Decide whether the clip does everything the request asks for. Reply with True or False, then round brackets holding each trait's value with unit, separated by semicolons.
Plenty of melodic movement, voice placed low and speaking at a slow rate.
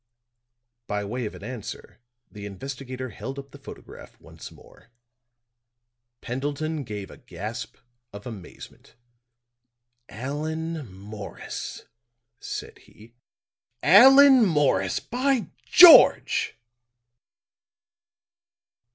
True (6.9 semitones; 130 Hz; 85 wpm)